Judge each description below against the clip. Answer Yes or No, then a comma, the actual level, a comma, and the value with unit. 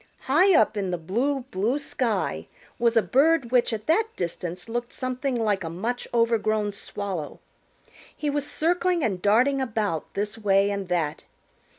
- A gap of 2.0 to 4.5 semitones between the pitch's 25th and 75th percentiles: No, average, 5.1 semitones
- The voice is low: No, high, 225 Hz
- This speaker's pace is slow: No, average, 160 wpm